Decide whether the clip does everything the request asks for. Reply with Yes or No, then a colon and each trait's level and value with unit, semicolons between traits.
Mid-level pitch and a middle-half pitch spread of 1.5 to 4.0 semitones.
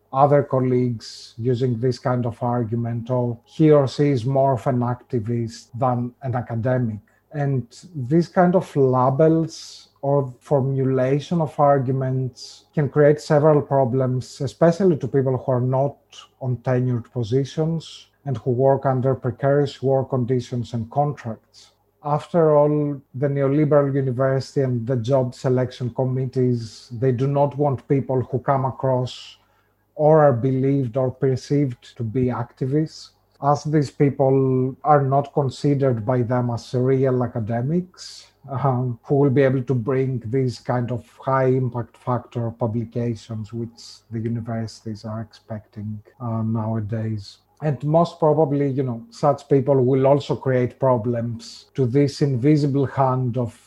No: low, 130 Hz; average, 2.8 semitones